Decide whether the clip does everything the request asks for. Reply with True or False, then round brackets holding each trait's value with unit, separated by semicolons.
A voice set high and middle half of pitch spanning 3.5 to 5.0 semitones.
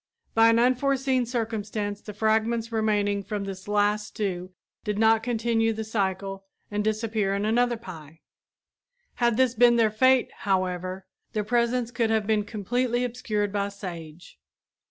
False (215 Hz; 2.7 semitones)